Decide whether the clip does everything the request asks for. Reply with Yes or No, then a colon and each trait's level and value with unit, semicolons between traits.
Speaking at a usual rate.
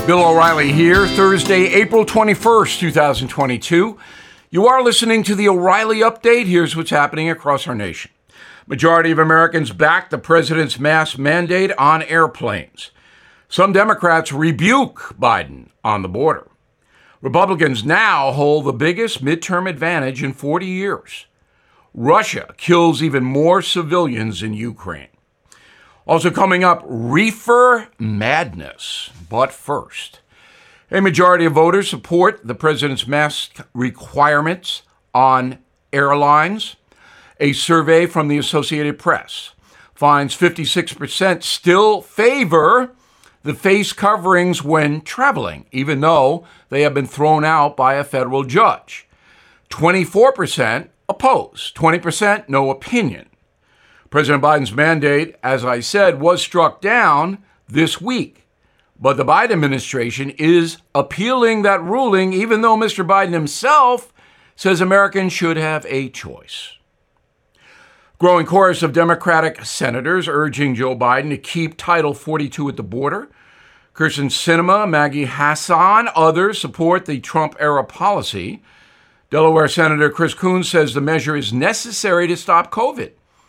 No: slow, 120 wpm